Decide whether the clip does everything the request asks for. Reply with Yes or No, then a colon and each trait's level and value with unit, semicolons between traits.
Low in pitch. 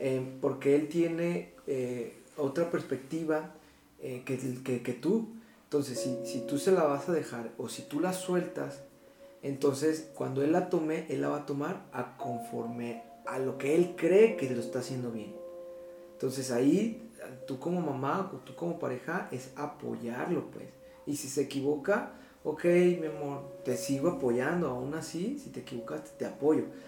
No: medium, 150 Hz